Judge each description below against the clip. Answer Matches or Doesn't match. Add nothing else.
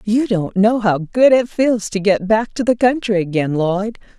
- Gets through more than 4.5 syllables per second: Doesn't match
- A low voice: Doesn't match